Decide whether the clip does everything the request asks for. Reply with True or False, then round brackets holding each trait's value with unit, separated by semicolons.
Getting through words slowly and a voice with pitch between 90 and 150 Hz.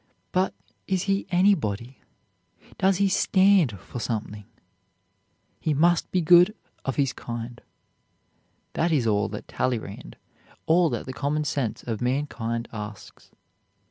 True (125 wpm; 140 Hz)